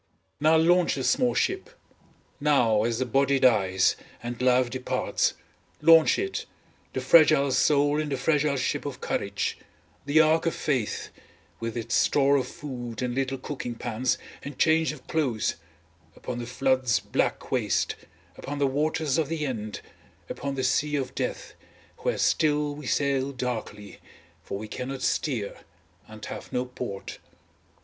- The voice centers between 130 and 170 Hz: Yes, low, 135 Hz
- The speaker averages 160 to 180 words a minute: No, average, 150 wpm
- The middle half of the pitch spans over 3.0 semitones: Yes, average, 3.6 semitones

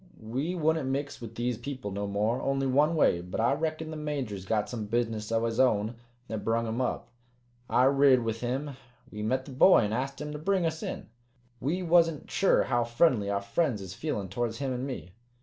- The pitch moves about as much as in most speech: Yes, average, 5.0 semitones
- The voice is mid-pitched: No, low, 125 Hz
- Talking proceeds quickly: Yes, fast, 210 wpm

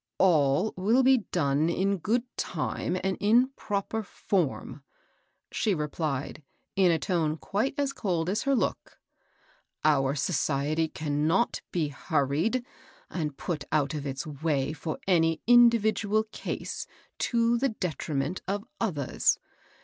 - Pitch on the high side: No, medium, 175 Hz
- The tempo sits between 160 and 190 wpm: No, slow, 135 wpm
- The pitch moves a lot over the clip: Yes, wide, 6.2 semitones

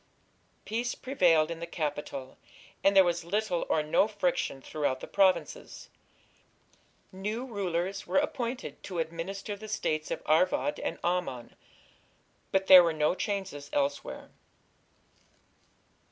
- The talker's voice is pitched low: No, medium, 180 Hz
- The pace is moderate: No, slow, 125 wpm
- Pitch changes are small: No, average, 4.7 semitones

